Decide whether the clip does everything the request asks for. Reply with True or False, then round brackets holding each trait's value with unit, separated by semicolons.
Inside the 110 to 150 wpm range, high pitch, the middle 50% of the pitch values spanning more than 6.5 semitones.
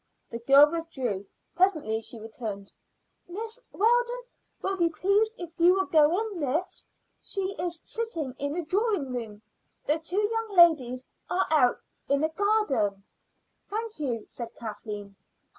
True (140 wpm; 325 Hz; 8.3 semitones)